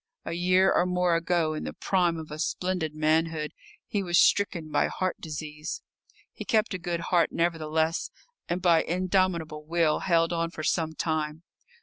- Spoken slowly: No, average, 165 wpm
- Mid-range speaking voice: Yes, medium, 165 Hz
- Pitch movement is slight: Yes, narrow, 2.3 semitones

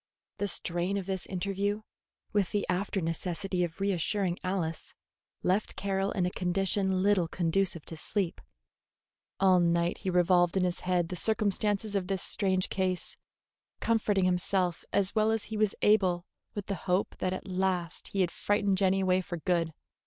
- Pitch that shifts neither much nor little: No, narrow, 2.0 semitones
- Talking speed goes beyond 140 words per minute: Yes, average, 165 wpm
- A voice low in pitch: No, medium, 185 Hz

